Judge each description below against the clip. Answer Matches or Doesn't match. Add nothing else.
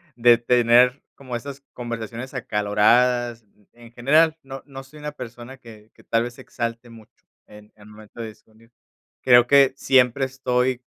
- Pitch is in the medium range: Doesn't match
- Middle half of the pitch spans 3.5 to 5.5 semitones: Doesn't match